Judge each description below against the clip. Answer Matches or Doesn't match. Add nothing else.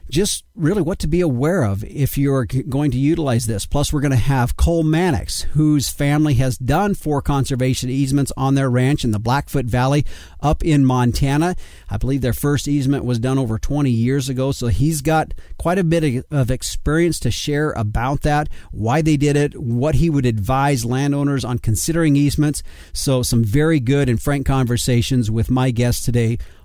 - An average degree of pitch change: Matches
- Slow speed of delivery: Doesn't match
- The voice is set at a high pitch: Doesn't match